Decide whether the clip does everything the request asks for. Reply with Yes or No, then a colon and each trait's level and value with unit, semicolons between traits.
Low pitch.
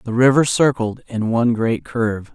Yes: low, 120 Hz